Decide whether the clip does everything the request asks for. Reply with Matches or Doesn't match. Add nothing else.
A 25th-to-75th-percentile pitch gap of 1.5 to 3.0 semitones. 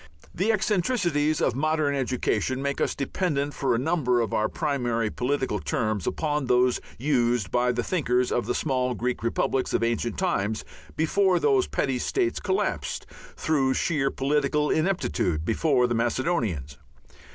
Doesn't match